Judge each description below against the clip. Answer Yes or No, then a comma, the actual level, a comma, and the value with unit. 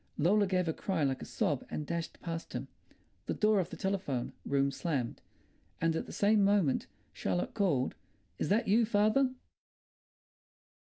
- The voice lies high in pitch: No, medium, 175 Hz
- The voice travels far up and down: Yes, wide, 6.0 semitones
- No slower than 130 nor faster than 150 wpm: No, average, 160 wpm